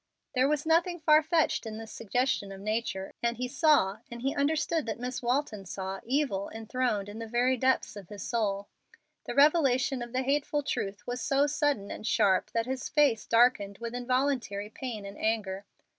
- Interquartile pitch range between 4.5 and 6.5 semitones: Yes, average, 4.8 semitones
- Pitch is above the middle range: Yes, high, 240 Hz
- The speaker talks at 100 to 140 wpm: No, average, 185 wpm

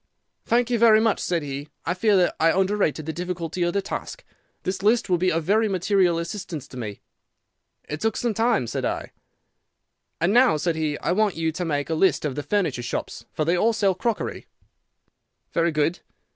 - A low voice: No, medium, 180 Hz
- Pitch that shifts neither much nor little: Yes, average, 4.7 semitones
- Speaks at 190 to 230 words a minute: Yes, average, 200 wpm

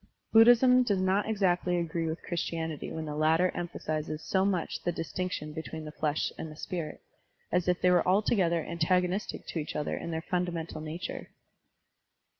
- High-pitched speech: No, medium, 170 Hz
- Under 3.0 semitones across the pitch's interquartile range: Yes, narrow, 2.5 semitones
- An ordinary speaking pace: Yes, average, 170 wpm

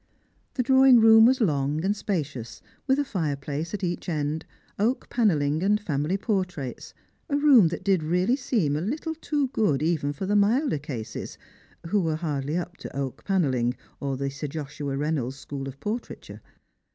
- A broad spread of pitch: Yes, wide, 7.0 semitones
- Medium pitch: Yes, medium, 165 Hz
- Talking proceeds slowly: No, average, 170 wpm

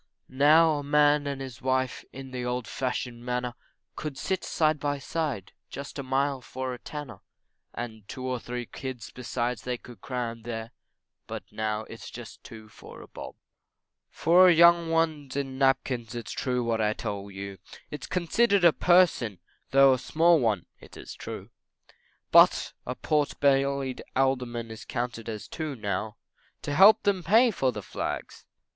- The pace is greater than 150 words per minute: Yes, average, 170 wpm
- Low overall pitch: Yes, low, 130 Hz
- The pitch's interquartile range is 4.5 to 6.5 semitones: No, average, 3.9 semitones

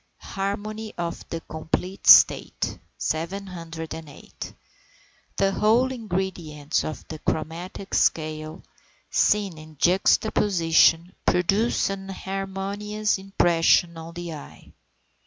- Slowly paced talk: Yes, slow, 90 wpm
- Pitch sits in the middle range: Yes, medium, 180 Hz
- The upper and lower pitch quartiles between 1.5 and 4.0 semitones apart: Yes, average, 3.4 semitones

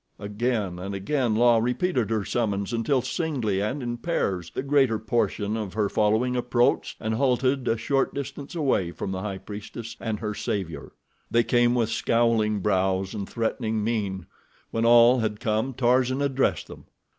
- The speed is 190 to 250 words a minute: No, average, 165 wpm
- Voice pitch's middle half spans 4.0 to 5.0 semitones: No, average, 3.3 semitones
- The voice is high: No, low, 115 Hz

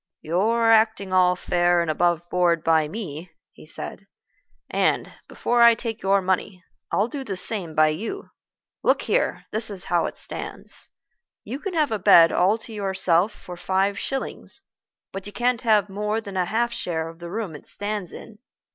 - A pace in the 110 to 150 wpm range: No, average, 175 wpm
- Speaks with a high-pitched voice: Yes, high, 195 Hz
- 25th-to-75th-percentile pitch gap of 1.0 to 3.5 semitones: No, average, 4.2 semitones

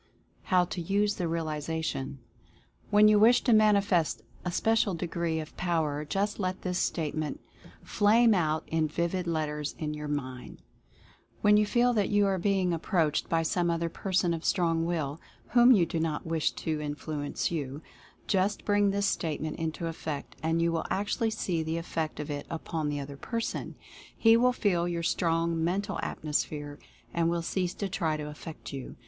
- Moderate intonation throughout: Yes, average, 4.0 semitones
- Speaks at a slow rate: No, average, 175 wpm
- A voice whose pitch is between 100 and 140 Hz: No, medium, 170 Hz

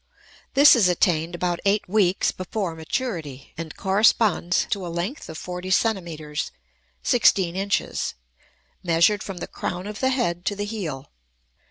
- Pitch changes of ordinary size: Yes, average, 3.5 semitones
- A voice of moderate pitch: Yes, medium, 180 Hz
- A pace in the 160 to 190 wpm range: No, average, 145 wpm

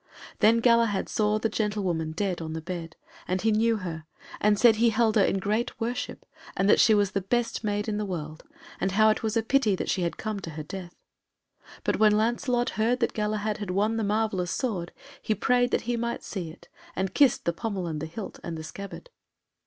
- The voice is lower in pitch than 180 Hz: No, high, 210 Hz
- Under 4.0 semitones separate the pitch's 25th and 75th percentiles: Yes, average, 3.6 semitones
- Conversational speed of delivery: No, fast, 220 wpm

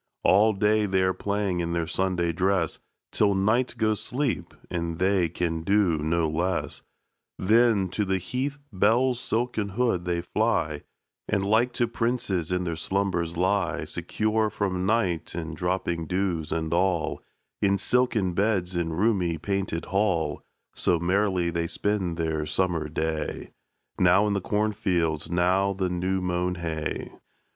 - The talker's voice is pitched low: Yes, very low, 95 Hz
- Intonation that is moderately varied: Yes, average, 3.4 semitones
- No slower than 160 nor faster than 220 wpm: No, average, 145 wpm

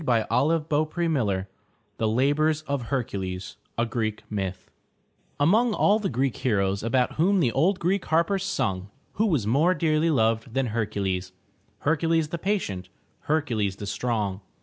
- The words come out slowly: No, average, 150 wpm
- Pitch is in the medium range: No, low, 130 Hz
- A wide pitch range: Yes, wide, 7.3 semitones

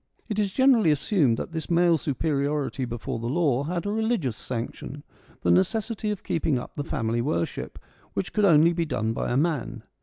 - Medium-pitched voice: Yes, medium, 155 Hz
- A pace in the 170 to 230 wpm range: Yes, average, 185 wpm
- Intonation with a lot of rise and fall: Yes, wide, 6.2 semitones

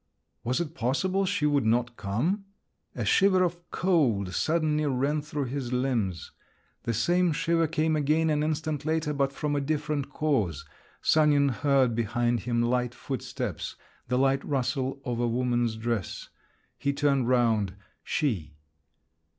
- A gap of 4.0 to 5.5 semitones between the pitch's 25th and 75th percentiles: Yes, average, 4.3 semitones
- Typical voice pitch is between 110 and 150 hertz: Yes, medium, 140 Hz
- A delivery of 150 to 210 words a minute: No, average, 140 wpm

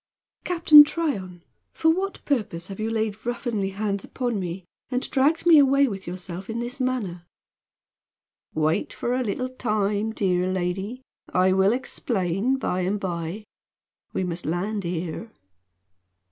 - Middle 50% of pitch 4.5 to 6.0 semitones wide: Yes, wide, 5.6 semitones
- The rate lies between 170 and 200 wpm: No, average, 140 wpm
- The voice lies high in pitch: Yes, high, 205 Hz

